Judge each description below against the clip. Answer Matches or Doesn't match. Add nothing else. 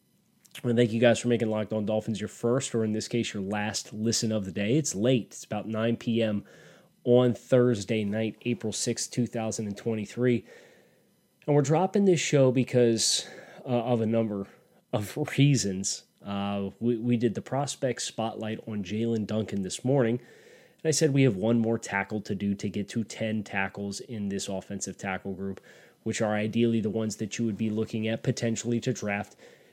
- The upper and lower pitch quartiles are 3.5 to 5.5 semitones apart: Doesn't match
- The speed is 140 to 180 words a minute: Doesn't match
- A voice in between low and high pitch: Doesn't match